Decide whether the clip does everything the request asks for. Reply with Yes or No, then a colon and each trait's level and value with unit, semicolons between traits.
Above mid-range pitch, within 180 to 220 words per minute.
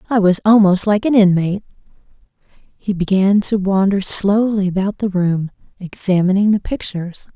No: high, 195 Hz; average, 140 wpm